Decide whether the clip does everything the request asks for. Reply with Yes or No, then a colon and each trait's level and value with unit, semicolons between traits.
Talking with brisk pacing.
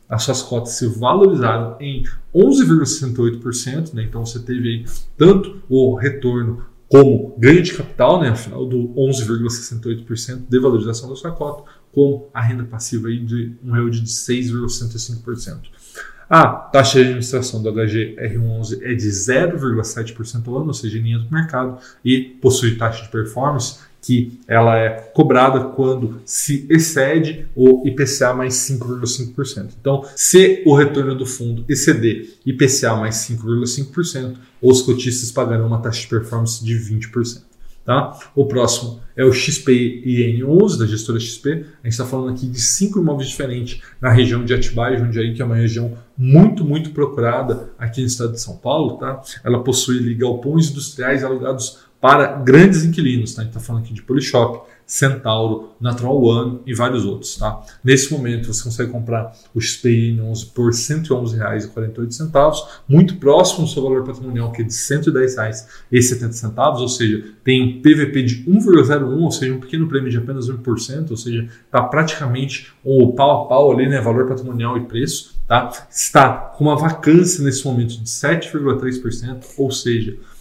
No: average, 155 wpm